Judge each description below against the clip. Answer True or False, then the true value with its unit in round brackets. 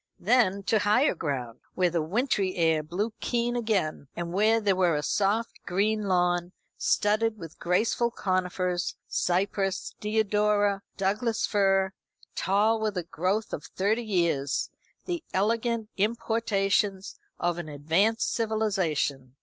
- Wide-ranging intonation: False (3.6 semitones)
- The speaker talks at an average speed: False (125 wpm)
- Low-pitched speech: False (195 Hz)